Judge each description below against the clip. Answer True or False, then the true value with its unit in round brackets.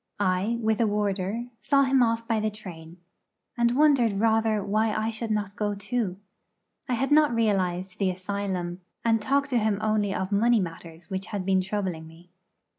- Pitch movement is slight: False (3.4 semitones)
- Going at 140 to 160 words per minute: False (180 wpm)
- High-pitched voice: True (210 Hz)